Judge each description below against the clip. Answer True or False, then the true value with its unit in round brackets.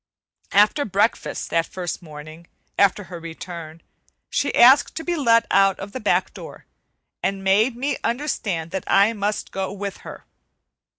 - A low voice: False (195 Hz)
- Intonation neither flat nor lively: True (4.9 semitones)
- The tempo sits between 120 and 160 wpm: True (155 wpm)